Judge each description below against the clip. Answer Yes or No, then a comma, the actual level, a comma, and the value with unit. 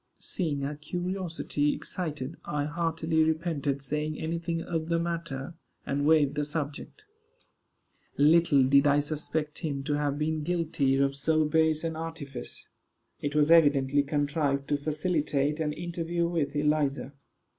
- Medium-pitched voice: Yes, medium, 150 Hz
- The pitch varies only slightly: Yes, narrow, 2.3 semitones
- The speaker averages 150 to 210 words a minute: No, average, 140 wpm